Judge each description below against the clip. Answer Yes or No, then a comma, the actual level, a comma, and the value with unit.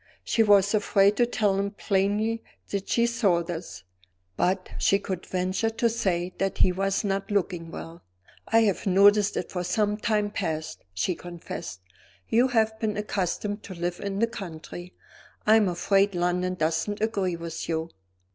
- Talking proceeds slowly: No, average, 165 wpm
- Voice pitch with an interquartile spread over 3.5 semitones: No, average, 2.9 semitones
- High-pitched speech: Yes, high, 195 Hz